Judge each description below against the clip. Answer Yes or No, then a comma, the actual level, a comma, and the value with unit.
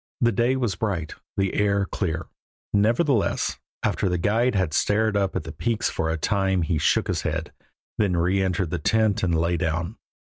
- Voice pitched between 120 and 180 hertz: No, very low, 95 Hz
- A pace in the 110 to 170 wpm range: No, average, 180 wpm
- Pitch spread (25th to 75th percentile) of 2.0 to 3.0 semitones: No, average, 4.0 semitones